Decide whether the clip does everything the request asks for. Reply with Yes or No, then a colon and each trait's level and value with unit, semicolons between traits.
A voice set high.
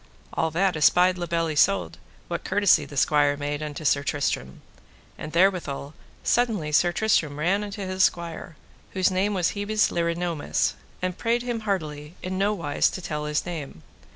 No: medium, 170 Hz